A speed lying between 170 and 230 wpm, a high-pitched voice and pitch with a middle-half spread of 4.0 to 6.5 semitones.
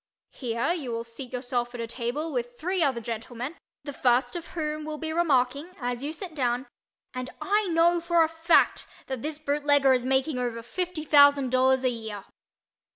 Yes: average, 185 wpm; very high, 270 Hz; average, 4.5 semitones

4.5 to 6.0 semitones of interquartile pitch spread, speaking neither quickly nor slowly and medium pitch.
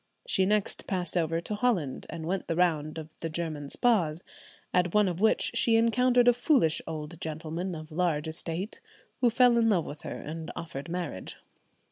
Yes: average, 4.9 semitones; average, 180 wpm; medium, 170 Hz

